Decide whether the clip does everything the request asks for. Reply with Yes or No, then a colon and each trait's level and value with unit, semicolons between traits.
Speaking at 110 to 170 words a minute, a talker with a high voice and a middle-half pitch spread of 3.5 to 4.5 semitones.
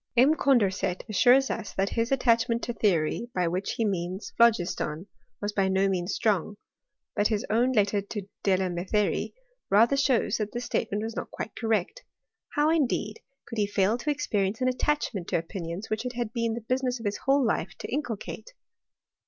No: average, 185 wpm; high, 215 Hz; average, 3.9 semitones